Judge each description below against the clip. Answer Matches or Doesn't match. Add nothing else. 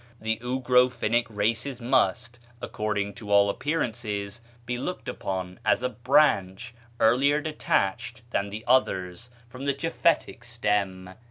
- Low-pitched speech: Matches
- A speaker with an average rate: Doesn't match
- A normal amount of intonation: Matches